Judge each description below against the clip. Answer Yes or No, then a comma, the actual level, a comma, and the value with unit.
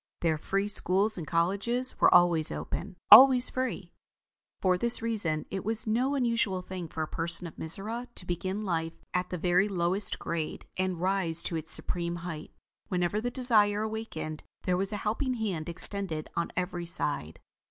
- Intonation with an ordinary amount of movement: Yes, average, 4.1 semitones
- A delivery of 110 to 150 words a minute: No, average, 170 wpm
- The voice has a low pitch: No, medium, 185 Hz